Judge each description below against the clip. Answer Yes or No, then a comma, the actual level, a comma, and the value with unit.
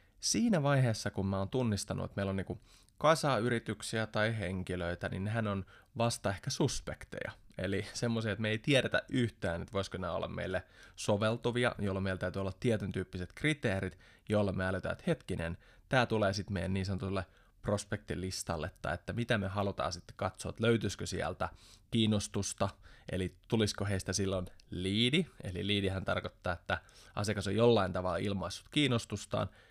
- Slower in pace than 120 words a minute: No, fast, 155 wpm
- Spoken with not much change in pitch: No, average, 3.3 semitones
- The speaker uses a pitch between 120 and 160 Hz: No, low, 100 Hz